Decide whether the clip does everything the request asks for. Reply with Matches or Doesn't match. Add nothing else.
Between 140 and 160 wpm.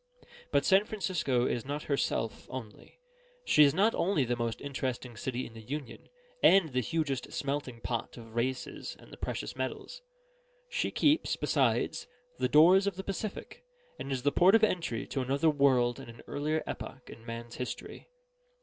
Doesn't match